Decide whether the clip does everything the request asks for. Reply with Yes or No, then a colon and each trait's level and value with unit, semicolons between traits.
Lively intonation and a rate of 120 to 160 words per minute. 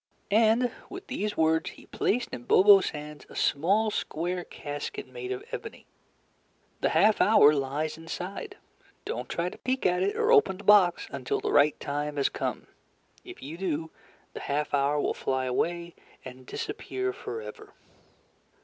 Yes: wide, 6.3 semitones; average, 155 wpm